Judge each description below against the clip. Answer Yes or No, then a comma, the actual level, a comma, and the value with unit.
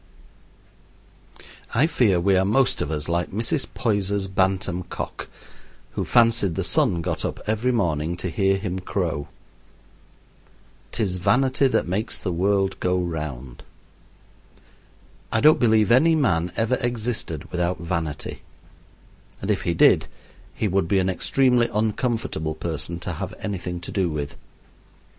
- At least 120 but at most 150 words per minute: Yes, average, 140 wpm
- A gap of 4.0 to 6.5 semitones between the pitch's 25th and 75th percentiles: Yes, average, 4.5 semitones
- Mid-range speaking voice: No, very low, 95 Hz